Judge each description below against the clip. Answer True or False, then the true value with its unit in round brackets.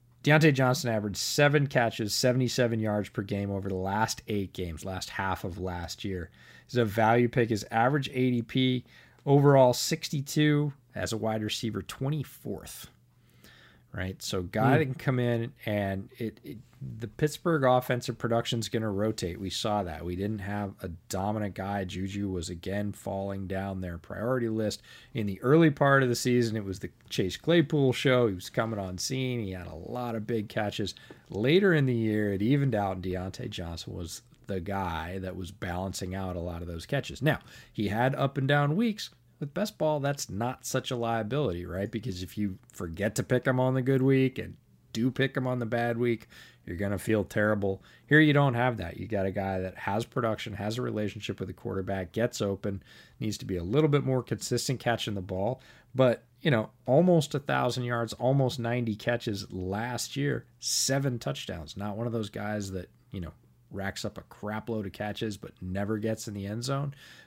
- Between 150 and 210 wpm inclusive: True (195 wpm)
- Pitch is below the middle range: True (110 Hz)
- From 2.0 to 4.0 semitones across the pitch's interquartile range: False (4.5 semitones)